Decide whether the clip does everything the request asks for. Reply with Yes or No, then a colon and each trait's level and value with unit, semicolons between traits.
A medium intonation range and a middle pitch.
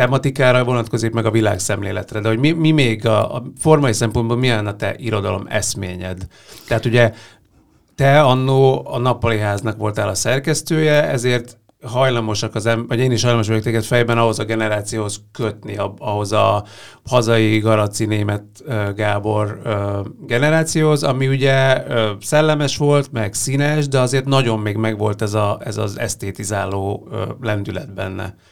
No: average, 3.5 semitones; low, 115 Hz